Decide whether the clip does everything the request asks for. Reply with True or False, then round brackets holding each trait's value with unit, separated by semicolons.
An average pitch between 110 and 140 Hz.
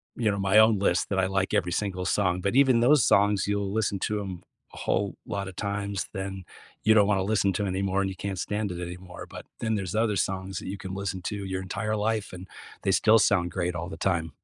False (100 Hz)